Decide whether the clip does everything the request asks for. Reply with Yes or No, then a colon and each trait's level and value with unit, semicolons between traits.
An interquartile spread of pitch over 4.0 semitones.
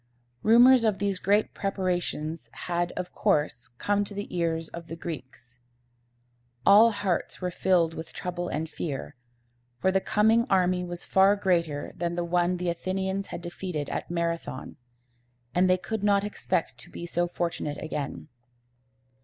No: average, 2.8 semitones